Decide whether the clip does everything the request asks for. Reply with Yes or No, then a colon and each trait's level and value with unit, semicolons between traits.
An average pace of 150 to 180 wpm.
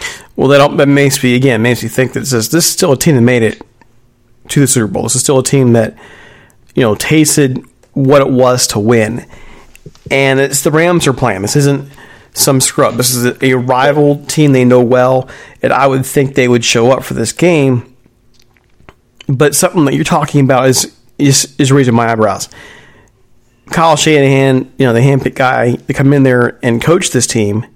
No: average, 200 wpm